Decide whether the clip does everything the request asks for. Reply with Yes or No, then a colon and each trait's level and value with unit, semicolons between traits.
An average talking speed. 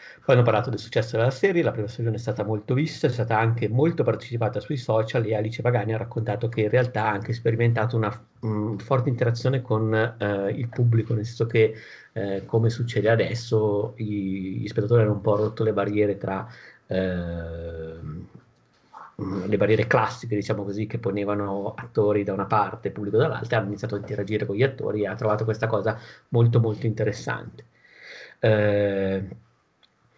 No: fast, 175 wpm